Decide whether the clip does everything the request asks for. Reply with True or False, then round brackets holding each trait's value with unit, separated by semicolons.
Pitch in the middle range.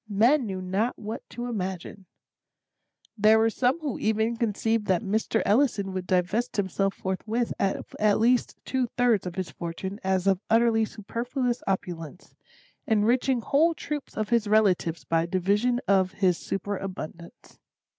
False (210 Hz)